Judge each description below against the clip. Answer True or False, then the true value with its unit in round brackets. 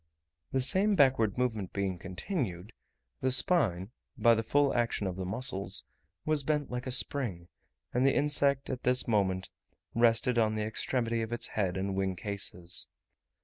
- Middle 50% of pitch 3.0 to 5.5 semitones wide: True (5.2 semitones)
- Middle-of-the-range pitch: False (115 Hz)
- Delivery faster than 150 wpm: True (160 wpm)